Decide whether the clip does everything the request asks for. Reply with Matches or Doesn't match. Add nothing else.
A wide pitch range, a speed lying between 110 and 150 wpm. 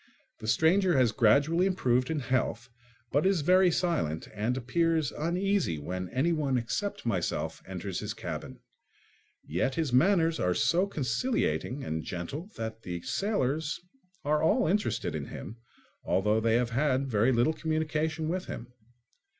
Matches